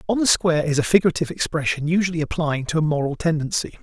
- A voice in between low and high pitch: Yes, medium, 160 Hz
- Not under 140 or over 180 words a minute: No, fast, 205 wpm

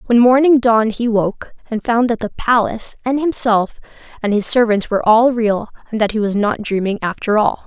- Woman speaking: Yes, female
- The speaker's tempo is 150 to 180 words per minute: No, fast, 205 wpm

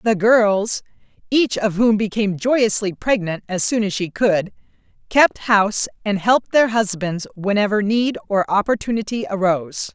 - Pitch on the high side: Yes, high, 205 Hz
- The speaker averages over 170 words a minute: No, slow, 135 wpm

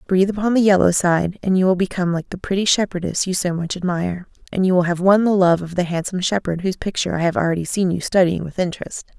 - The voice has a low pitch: No, medium, 185 Hz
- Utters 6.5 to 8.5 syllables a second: Yes, 6.8 syllables/s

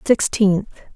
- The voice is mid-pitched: No, high, 205 Hz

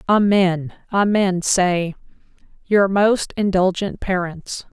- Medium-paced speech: No, slow, 90 wpm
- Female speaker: Yes, female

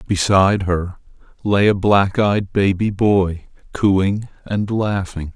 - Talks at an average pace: No, slow, 125 wpm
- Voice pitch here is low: Yes, low, 100 Hz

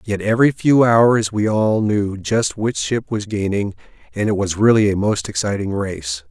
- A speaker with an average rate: Yes, average, 190 wpm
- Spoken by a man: Yes, male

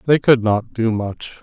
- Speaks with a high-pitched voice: No, low, 115 Hz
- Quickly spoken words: Yes, fast, 210 wpm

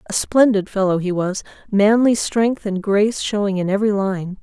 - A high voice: Yes, high, 205 Hz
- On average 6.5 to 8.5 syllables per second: No, 5.1 syllables/s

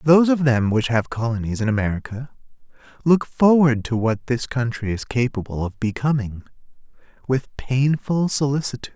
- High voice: No, low, 125 Hz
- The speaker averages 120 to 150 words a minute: Yes, average, 140 wpm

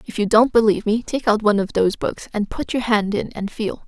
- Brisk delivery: Yes, fast, 280 wpm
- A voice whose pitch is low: No, high, 215 Hz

